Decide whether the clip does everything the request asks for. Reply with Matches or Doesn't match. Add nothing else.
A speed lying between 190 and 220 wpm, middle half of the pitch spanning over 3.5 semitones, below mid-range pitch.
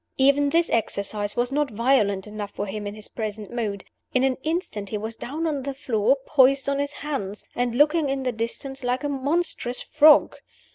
Doesn't match